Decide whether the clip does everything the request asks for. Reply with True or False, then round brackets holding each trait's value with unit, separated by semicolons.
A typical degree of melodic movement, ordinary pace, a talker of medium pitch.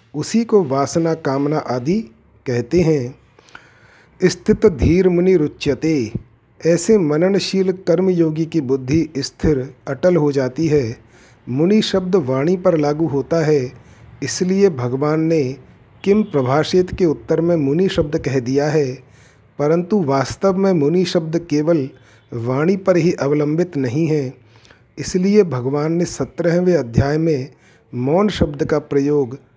True (4.7 semitones; 130 wpm; 155 Hz)